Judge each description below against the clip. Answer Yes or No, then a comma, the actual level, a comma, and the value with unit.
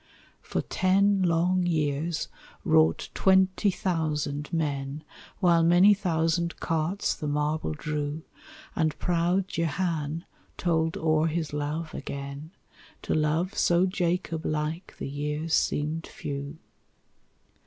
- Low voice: No, medium, 160 Hz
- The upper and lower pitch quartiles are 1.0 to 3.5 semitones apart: Yes, average, 2.9 semitones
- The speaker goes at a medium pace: No, slow, 110 wpm